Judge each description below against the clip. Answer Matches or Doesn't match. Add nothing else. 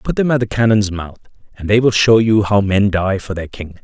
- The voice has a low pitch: Matches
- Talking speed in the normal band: Doesn't match